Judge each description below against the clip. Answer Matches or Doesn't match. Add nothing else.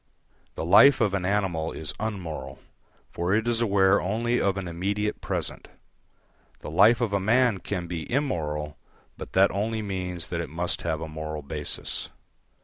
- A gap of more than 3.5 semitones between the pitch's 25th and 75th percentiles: Matches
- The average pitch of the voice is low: Matches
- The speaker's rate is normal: Matches